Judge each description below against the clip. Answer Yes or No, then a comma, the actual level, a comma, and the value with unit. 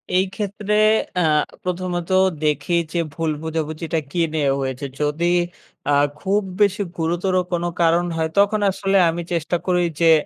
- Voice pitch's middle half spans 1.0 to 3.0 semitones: Yes, narrow, 2.6 semitones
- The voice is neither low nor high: Yes, medium, 170 Hz